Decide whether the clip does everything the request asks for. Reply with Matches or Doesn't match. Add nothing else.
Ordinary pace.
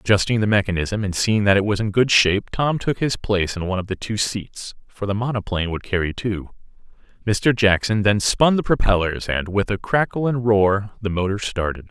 Doesn't match